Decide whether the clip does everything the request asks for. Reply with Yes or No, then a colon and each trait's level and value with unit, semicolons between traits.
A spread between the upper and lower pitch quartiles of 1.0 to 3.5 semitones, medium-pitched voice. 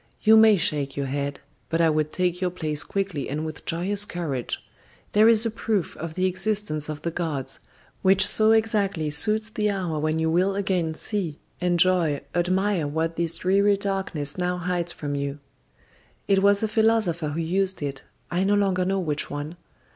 No: average, 4.3 semitones; medium, 180 Hz